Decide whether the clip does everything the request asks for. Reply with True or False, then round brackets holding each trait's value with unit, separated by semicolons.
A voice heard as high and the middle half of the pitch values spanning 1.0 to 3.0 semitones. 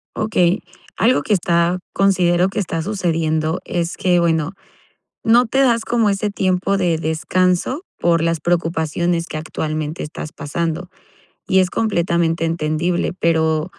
False (175 Hz; 2.7 semitones)